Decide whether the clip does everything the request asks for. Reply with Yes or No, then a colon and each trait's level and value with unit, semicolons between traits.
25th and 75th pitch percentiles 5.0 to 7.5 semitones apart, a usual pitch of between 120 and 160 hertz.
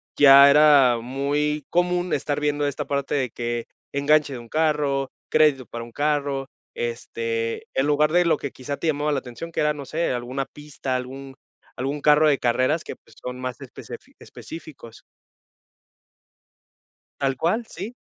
No: average, 2.8 semitones; medium, 140 Hz